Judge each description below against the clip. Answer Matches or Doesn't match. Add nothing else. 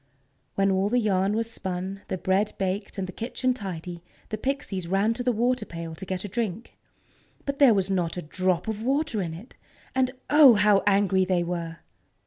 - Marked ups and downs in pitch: Doesn't match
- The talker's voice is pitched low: Doesn't match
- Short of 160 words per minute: Doesn't match